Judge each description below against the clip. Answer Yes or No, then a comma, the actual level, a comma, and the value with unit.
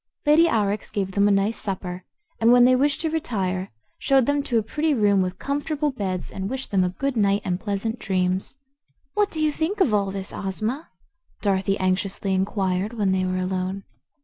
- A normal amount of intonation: No, wide, 5.8 semitones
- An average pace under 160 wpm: No, average, 195 wpm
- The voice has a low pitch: No, high, 200 Hz